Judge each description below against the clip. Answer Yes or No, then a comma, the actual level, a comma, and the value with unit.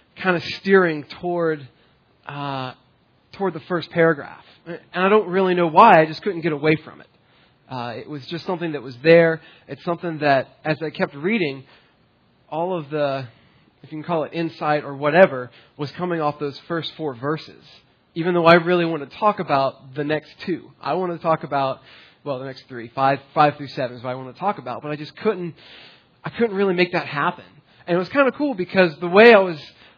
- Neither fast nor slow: No, fast, 215 wpm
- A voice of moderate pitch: Yes, medium, 155 Hz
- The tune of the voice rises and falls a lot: No, average, 4.0 semitones